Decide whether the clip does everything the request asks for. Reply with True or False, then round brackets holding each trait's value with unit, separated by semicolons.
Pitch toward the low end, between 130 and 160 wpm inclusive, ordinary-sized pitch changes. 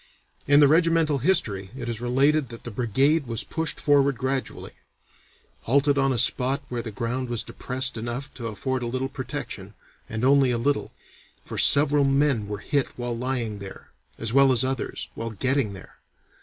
False (130 Hz; 175 wpm; 3.2 semitones)